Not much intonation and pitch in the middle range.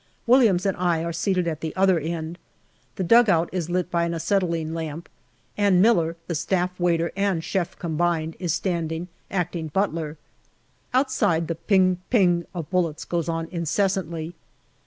Yes: narrow, 2.3 semitones; medium, 170 Hz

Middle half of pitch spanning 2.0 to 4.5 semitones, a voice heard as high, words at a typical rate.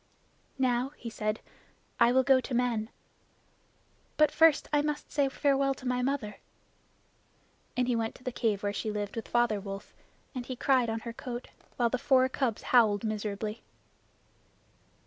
Yes: average, 3.2 semitones; high, 245 Hz; average, 165 wpm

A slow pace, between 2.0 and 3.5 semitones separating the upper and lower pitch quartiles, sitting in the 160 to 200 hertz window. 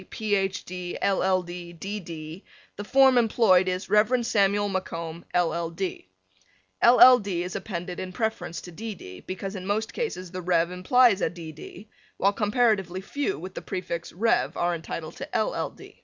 No: average, 175 wpm; average, 3.2 semitones; medium, 185 Hz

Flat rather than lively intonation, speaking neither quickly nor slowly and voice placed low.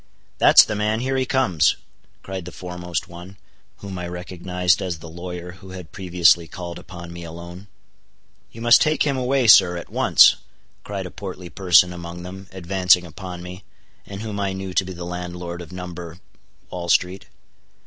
Yes: narrow, 1.7 semitones; average, 170 wpm; very low, 90 Hz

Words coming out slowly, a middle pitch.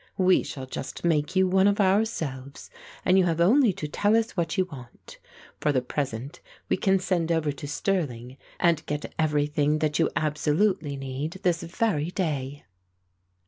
No: average, 165 wpm; medium, 160 Hz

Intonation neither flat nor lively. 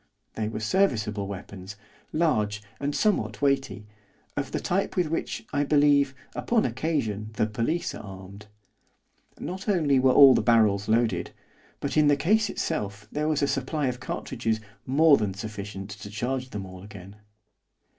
No: wide, 6.0 semitones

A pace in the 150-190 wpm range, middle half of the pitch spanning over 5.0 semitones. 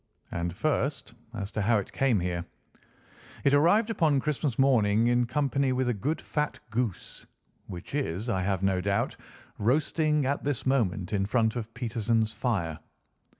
Yes: average, 155 wpm; wide, 5.6 semitones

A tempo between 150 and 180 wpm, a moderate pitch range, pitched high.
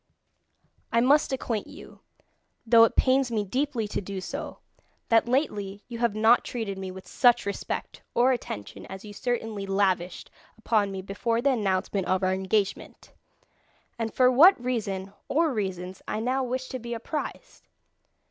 Yes: average, 155 wpm; average, 4.3 semitones; high, 225 Hz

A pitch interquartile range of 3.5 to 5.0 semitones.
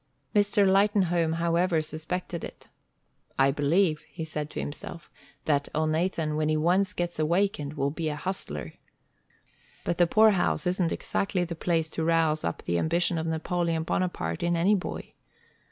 No: narrow, 2.6 semitones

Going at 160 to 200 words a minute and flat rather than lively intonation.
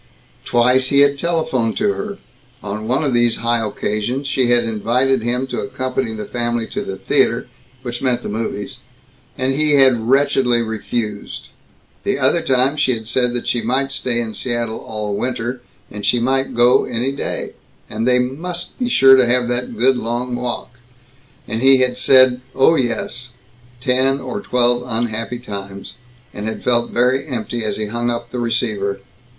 Yes: average, 175 wpm; narrow, 2.3 semitones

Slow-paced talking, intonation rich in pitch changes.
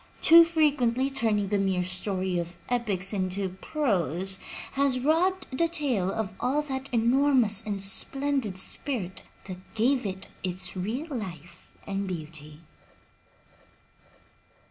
Yes: slow, 120 wpm; wide, 6.4 semitones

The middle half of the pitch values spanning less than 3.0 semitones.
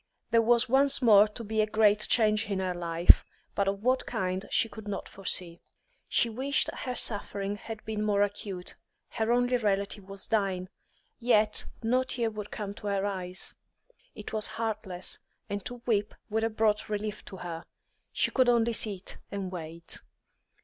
Yes: narrow, 2.5 semitones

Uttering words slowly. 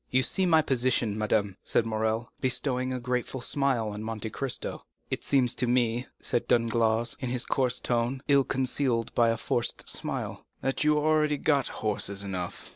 No: average, 175 wpm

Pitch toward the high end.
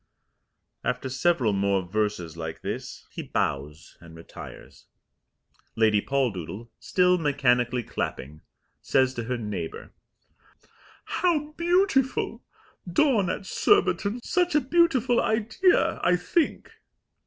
No: low, 130 Hz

